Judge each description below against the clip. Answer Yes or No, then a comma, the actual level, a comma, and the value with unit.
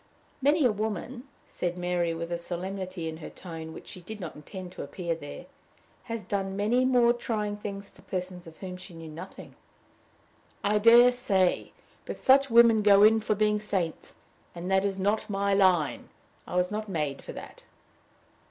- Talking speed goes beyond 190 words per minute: No, average, 180 wpm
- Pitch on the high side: Yes, high, 195 Hz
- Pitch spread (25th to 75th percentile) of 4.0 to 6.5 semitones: No, average, 3.5 semitones